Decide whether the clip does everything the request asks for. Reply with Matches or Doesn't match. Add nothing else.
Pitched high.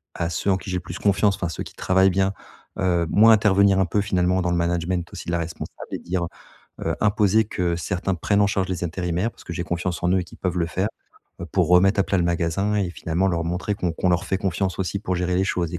Doesn't match